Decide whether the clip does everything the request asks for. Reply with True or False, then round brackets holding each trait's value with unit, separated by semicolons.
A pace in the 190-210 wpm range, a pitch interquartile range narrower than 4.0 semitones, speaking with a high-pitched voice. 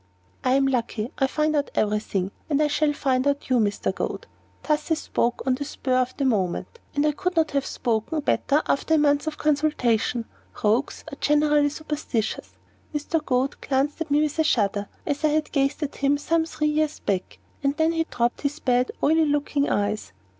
True (200 wpm; 3.3 semitones; 285 Hz)